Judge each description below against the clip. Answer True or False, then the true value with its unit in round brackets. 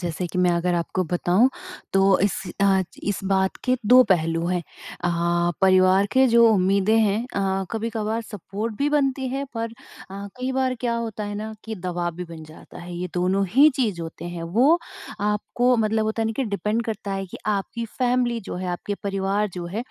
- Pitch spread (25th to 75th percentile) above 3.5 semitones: True (4.0 semitones)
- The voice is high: True (205 Hz)